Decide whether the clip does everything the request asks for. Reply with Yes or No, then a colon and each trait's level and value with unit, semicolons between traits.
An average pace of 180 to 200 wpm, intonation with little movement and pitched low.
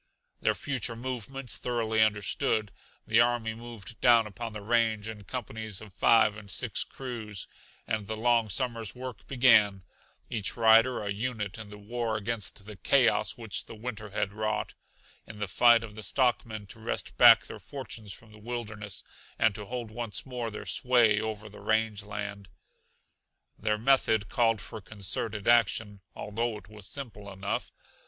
No: average, 160 wpm; narrow, 2.3 semitones; low, 110 Hz